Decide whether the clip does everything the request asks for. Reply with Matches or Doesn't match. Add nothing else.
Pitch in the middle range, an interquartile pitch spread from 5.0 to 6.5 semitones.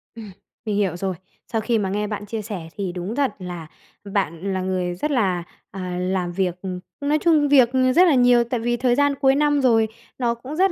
Doesn't match